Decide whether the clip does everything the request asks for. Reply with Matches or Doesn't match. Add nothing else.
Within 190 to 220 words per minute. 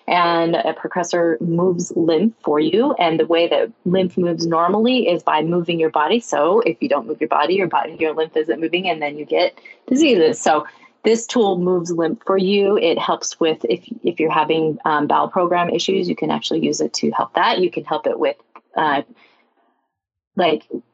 Matches